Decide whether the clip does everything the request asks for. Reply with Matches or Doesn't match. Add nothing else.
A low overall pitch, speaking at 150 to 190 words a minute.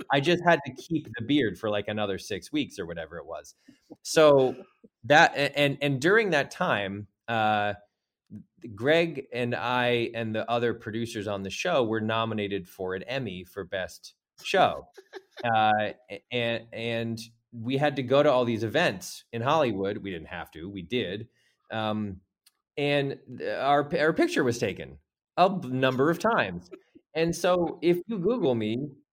Matches